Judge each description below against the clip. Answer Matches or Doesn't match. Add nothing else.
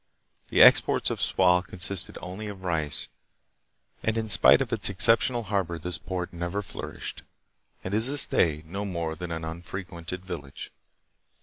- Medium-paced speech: Matches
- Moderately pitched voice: Doesn't match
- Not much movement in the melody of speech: Doesn't match